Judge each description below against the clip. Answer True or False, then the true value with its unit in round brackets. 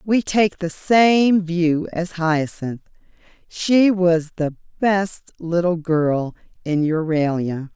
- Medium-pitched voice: True (170 Hz)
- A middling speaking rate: False (115 wpm)